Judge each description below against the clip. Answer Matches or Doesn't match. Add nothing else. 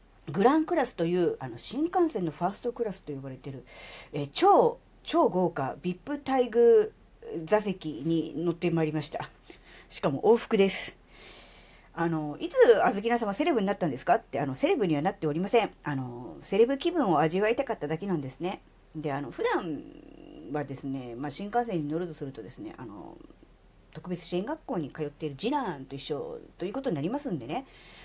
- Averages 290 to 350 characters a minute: Doesn't match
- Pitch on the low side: Doesn't match